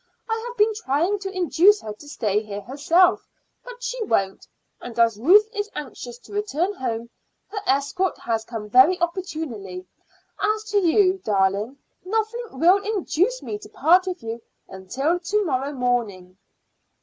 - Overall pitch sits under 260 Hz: No, very high, 320 Hz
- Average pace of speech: Yes, average, 155 wpm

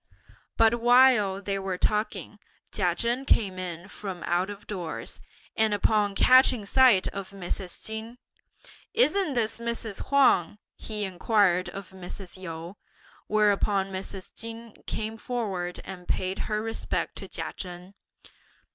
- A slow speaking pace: Yes, slow, 130 wpm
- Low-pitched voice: No, high, 205 Hz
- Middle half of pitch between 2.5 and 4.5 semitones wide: Yes, average, 3.3 semitones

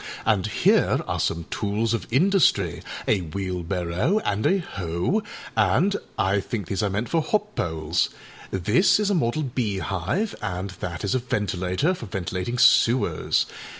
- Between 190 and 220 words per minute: No, average, 150 wpm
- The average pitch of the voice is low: Yes, low, 105 Hz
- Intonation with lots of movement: Yes, wide, 6.0 semitones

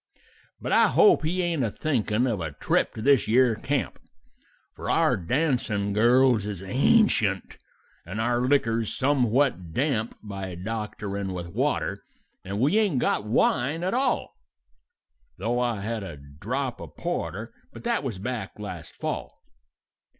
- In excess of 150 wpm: No, average, 145 wpm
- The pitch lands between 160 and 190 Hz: No, low, 115 Hz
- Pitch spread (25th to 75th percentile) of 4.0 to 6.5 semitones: Yes, average, 5.2 semitones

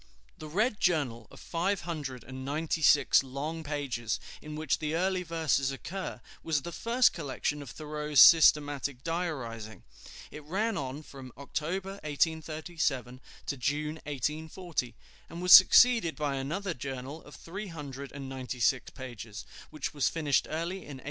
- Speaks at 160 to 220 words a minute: No, average, 150 wpm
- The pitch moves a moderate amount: Yes, average, 3.8 semitones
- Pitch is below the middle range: No, medium, 150 Hz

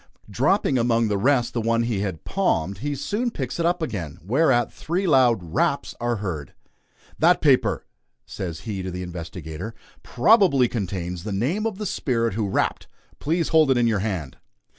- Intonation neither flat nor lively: No, wide, 7.1 semitones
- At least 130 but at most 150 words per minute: No, average, 175 wpm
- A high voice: No, low, 115 Hz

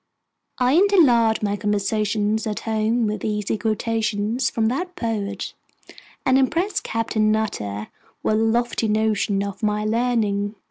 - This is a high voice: Yes, high, 220 Hz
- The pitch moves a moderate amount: No, narrow, 2.1 semitones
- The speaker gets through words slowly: Yes, slow, 130 wpm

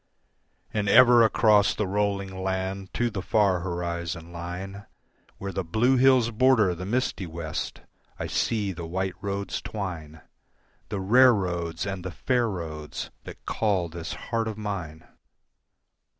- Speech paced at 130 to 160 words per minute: Yes, average, 140 wpm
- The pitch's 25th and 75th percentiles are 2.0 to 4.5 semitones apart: Yes, average, 3.8 semitones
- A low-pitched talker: Yes, very low, 95 Hz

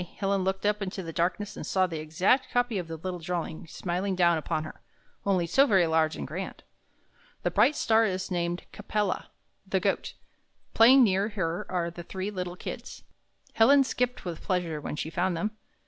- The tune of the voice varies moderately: Yes, average, 3.4 semitones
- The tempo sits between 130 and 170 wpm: No, average, 195 wpm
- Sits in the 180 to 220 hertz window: Yes, medium, 185 Hz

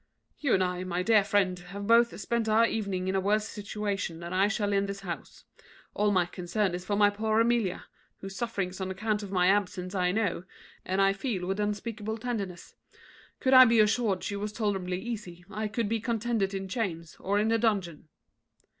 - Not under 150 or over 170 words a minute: No, average, 200 wpm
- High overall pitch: Yes, high, 200 Hz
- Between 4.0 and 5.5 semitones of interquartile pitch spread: No, average, 2.8 semitones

